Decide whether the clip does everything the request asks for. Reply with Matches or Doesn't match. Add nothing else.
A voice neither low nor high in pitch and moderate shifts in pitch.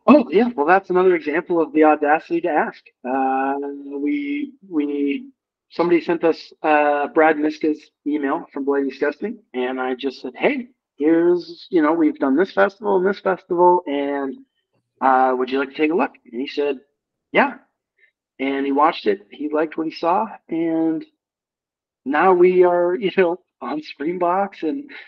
Doesn't match